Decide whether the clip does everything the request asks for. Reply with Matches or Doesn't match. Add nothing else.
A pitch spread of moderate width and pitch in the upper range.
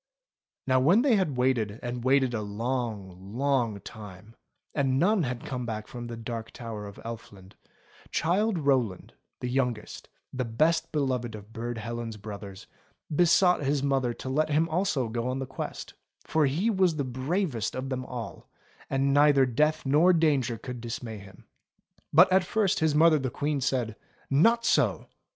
Doesn't match